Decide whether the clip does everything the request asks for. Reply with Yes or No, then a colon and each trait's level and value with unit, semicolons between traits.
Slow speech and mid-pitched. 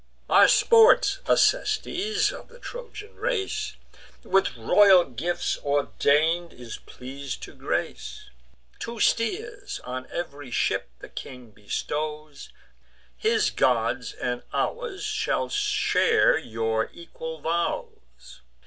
Yes: slow, 105 wpm; medium, 175 Hz